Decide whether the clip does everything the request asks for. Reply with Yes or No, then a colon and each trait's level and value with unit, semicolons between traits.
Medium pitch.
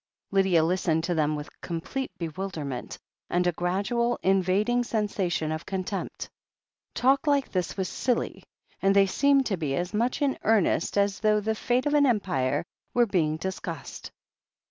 No: high, 195 Hz